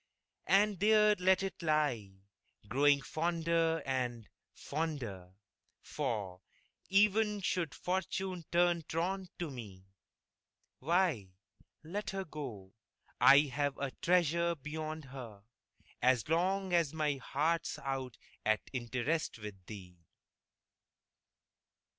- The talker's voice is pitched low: No, medium, 155 Hz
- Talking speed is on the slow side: Yes, slow, 100 wpm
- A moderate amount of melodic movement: No, wide, 5.9 semitones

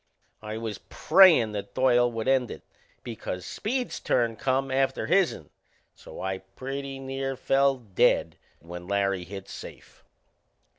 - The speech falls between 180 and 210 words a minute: No, slow, 135 wpm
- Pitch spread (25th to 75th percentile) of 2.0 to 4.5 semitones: No, average, 5.2 semitones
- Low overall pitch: Yes, low, 120 Hz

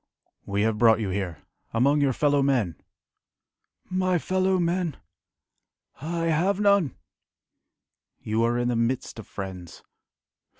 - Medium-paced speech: No, slow, 125 wpm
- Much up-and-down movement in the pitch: Yes, wide, 7.7 semitones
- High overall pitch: No, low, 135 Hz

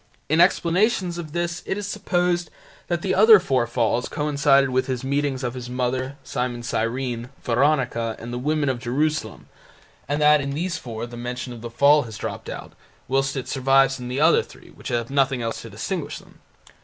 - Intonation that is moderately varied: Yes, average, 3.9 semitones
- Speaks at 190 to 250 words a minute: Yes, average, 195 wpm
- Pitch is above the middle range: No, low, 135 Hz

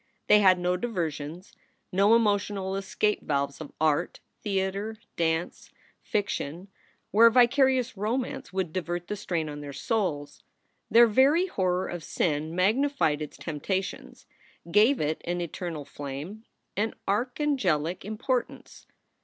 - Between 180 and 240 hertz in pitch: Yes, high, 190 Hz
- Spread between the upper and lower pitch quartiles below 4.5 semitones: No, wide, 5.4 semitones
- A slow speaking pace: Yes, slow, 120 wpm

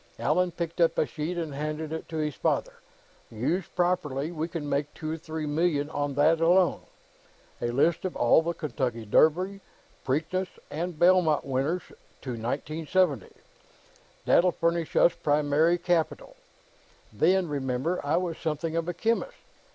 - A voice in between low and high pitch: Yes, medium, 160 Hz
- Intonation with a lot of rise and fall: No, average, 3.2 semitones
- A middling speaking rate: Yes, average, 150 wpm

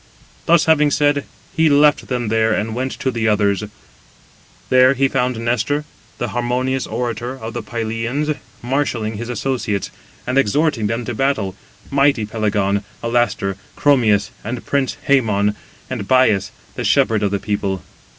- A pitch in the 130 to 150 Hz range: No, low, 120 Hz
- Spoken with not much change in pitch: No, average, 3.8 semitones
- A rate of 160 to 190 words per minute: No, average, 145 wpm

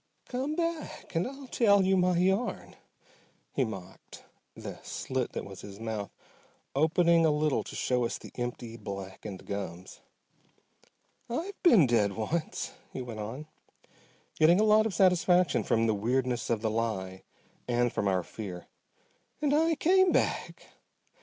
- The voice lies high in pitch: No, low, 130 Hz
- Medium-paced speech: Yes, average, 145 wpm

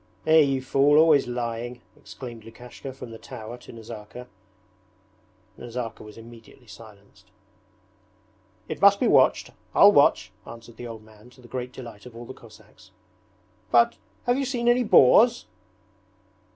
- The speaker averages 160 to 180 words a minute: No, average, 145 wpm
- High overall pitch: No, low, 120 Hz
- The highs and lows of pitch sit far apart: No, average, 2.8 semitones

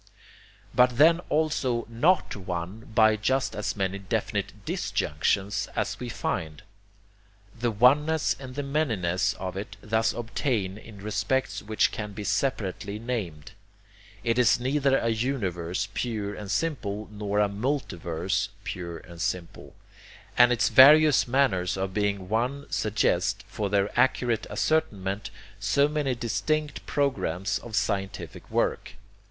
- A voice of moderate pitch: No, low, 110 Hz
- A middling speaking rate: No, slow, 130 wpm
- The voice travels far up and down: No, average, 4.9 semitones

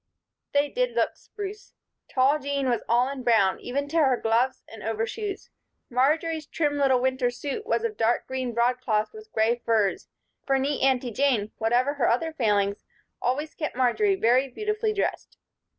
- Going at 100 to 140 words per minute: No, average, 165 wpm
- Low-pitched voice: No, very high, 260 Hz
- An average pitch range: Yes, average, 4.2 semitones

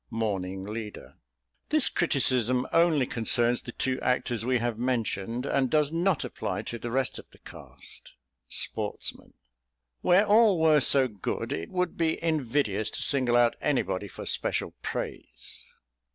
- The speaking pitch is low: Yes, low, 125 Hz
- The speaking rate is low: No, average, 145 wpm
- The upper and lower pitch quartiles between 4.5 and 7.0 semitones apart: Yes, average, 5.1 semitones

